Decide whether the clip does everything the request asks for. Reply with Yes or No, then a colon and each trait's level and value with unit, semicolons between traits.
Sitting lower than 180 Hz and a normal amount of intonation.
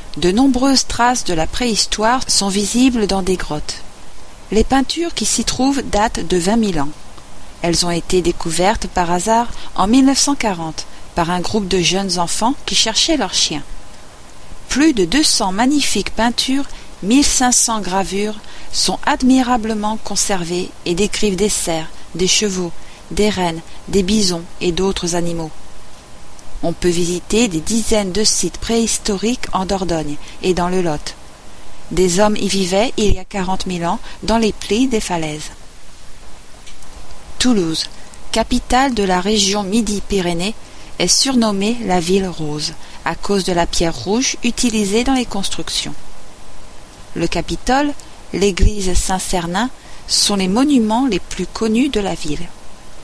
No: high, 200 Hz; average, 4.5 semitones